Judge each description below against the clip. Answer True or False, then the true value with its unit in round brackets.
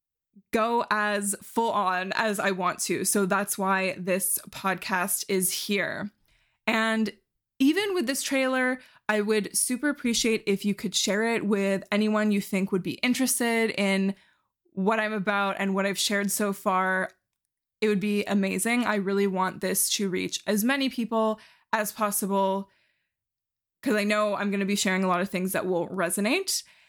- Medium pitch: False (205 Hz)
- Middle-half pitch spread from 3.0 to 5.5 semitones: False (2.4 semitones)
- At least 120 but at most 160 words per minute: False (170 wpm)